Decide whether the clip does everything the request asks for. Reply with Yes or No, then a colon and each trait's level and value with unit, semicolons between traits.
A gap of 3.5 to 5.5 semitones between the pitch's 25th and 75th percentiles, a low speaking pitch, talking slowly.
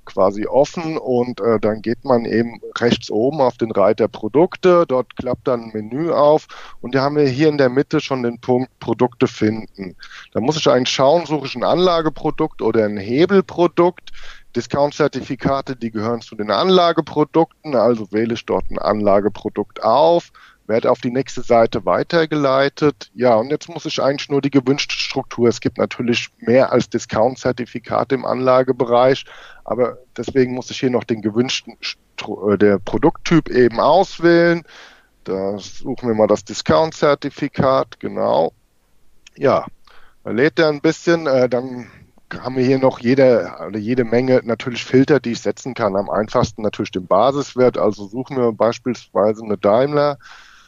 No: average, 3.9 semitones; low, 130 Hz; average, 155 wpm